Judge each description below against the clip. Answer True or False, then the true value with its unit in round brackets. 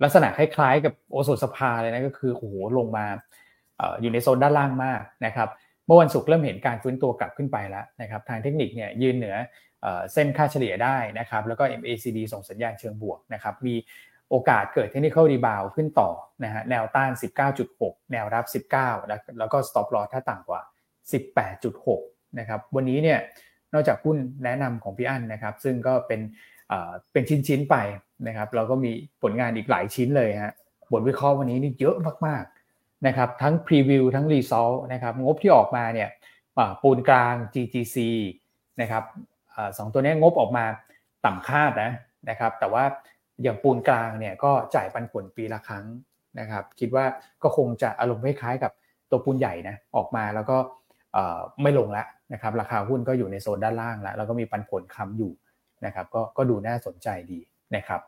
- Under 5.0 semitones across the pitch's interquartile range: True (3.5 semitones)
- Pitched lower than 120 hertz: False (125 Hz)